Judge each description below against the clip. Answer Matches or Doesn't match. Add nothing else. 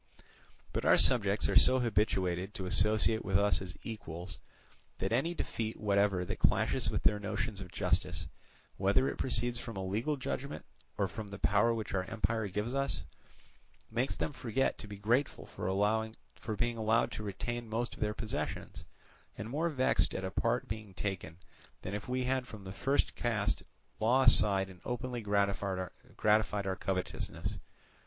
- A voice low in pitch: Matches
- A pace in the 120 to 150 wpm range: Doesn't match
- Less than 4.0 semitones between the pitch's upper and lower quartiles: Matches